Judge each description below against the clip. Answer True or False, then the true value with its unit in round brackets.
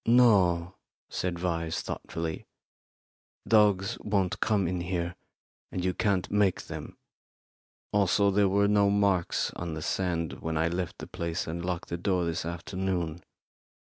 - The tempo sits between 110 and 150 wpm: True (140 wpm)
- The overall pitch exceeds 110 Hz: False (90 Hz)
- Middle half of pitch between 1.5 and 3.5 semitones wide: True (2.9 semitones)